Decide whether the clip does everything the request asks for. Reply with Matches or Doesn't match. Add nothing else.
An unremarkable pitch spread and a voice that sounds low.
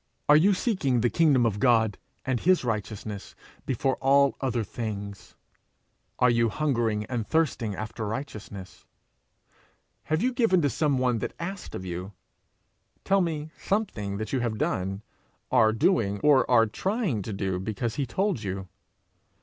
Doesn't match